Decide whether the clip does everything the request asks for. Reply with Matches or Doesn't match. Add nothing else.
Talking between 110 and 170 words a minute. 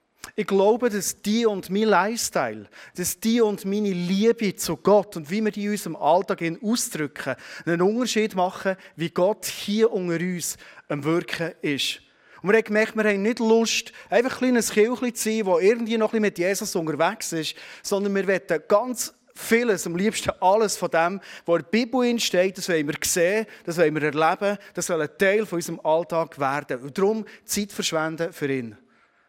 Doesn't match